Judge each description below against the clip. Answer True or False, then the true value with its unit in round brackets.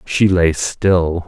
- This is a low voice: True (90 Hz)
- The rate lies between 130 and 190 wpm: True (140 wpm)